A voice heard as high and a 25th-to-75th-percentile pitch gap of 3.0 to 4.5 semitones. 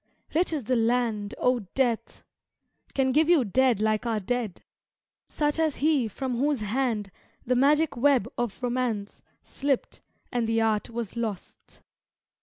Yes: high, 245 Hz; average, 3.5 semitones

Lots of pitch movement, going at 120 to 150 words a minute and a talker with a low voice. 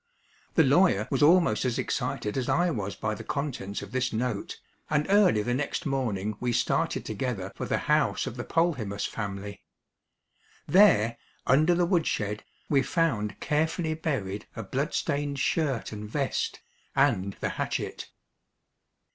Yes: wide, 6.9 semitones; average, 145 wpm; low, 130 Hz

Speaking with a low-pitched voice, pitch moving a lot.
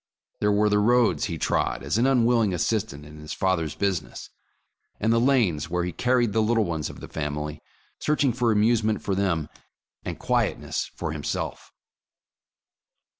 Yes: low, 105 Hz; wide, 6.0 semitones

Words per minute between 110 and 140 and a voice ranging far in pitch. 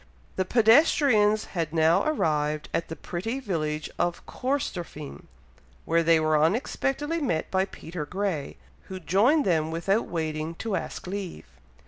Yes: slow, 135 wpm; wide, 5.7 semitones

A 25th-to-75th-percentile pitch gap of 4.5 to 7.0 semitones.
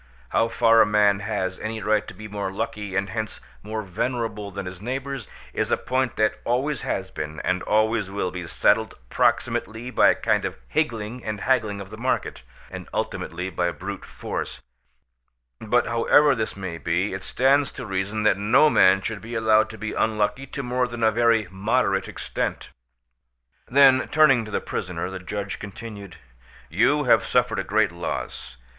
No: average, 3.5 semitones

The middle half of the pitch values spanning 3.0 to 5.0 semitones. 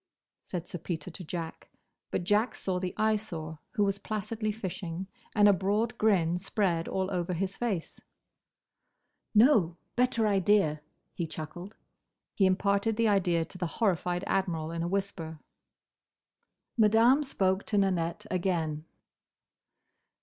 Yes: average, 3.5 semitones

